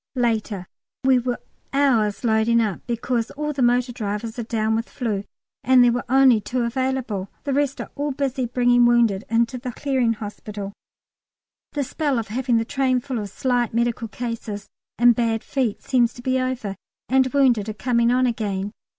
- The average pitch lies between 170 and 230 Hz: No, high, 240 Hz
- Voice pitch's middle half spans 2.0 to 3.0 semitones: Yes, average, 2.7 semitones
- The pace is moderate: Yes, average, 180 wpm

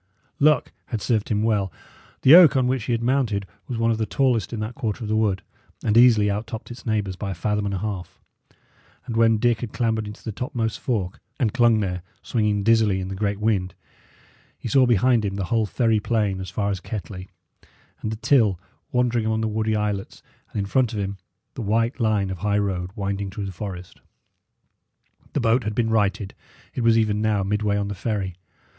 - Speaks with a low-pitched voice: Yes, low, 110 Hz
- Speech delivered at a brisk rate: Yes, fast, 210 wpm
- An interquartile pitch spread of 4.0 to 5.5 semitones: No, narrow, 2.4 semitones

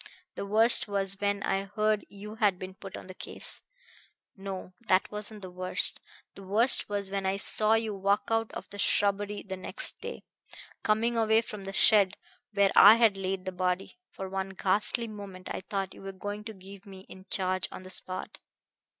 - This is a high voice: Yes, high, 200 Hz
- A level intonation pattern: Yes, narrow, 1.8 semitones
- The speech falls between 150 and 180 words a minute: No, average, 195 wpm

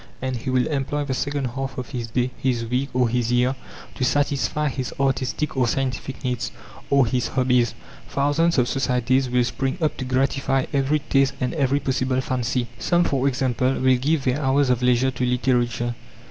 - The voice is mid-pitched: No, low, 130 Hz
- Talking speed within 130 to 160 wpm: No, average, 185 wpm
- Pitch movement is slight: Yes, narrow, 1.6 semitones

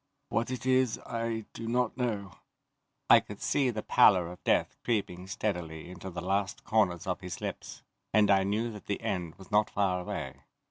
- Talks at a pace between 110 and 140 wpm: No, average, 185 wpm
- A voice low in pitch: Yes, low, 100 Hz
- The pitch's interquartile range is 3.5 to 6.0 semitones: Yes, average, 4.0 semitones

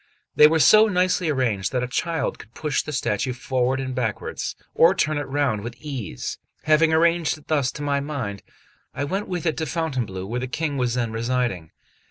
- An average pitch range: Yes, average, 4.5 semitones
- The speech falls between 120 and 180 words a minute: No, average, 200 wpm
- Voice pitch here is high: No, medium, 140 Hz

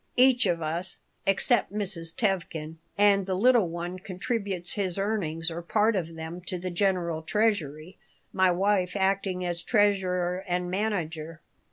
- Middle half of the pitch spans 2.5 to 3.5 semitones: Yes, average, 2.9 semitones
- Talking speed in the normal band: Yes, average, 145 wpm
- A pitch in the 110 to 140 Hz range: No, medium, 185 Hz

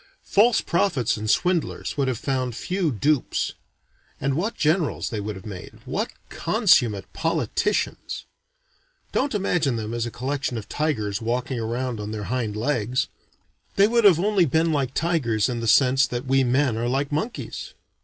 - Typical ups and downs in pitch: No, wide, 5.9 semitones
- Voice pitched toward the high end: No, low, 130 Hz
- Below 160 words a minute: No, average, 165 wpm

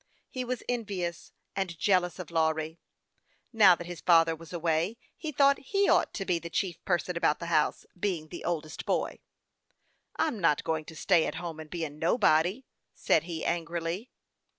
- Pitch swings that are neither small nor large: Yes, average, 3.1 semitones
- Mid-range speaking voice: Yes, medium, 170 Hz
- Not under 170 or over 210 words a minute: Yes, average, 180 wpm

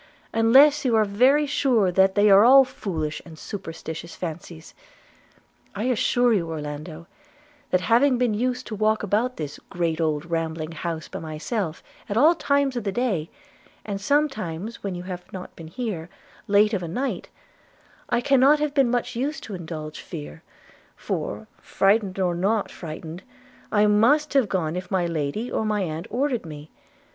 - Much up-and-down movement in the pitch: Yes, wide, 6.7 semitones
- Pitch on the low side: No, high, 200 Hz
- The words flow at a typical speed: Yes, average, 165 wpm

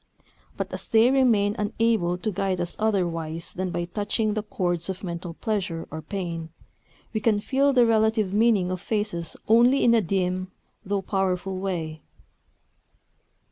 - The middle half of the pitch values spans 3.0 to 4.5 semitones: Yes, average, 3.8 semitones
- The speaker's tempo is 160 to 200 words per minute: No, average, 150 wpm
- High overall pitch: Yes, high, 195 Hz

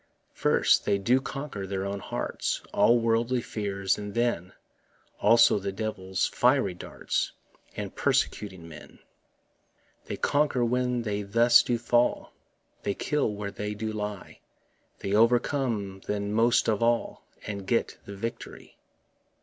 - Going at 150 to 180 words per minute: No, slow, 135 wpm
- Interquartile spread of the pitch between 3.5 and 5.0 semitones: No, average, 3.1 semitones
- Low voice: Yes, low, 105 Hz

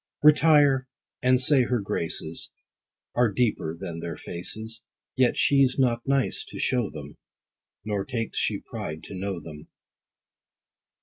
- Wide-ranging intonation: Yes, wide, 6.8 semitones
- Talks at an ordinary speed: No, slow, 130 wpm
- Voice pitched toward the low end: Yes, low, 115 Hz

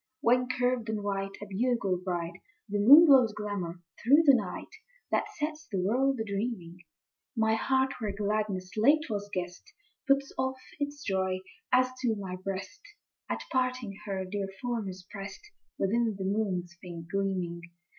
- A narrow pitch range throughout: No, average, 5.0 semitones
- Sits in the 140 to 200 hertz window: No, high, 210 Hz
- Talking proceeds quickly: No, average, 160 wpm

